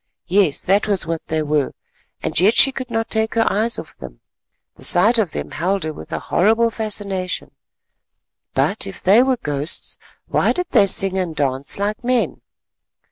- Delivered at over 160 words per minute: Yes, average, 175 wpm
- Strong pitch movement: Yes, wide, 5.9 semitones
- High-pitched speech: Yes, high, 195 Hz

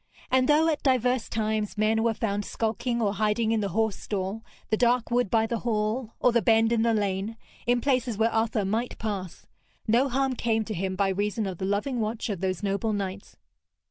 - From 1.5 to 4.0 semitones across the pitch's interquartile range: Yes, narrow, 2.5 semitones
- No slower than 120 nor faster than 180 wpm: No, fast, 205 wpm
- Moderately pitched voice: No, high, 220 Hz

